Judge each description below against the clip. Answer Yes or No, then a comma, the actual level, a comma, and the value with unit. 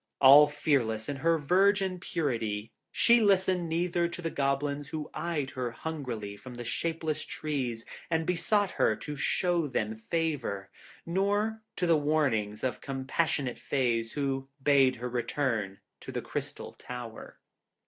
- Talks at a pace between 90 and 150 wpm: Yes, average, 140 wpm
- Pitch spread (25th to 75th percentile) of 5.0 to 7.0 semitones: Yes, wide, 5.4 semitones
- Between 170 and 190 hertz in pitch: No, medium, 145 Hz